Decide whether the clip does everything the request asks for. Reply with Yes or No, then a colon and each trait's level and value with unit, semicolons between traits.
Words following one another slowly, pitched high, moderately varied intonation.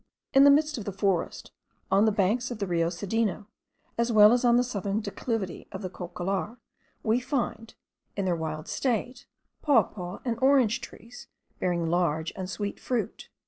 No: average, 170 wpm; high, 210 Hz; average, 4.7 semitones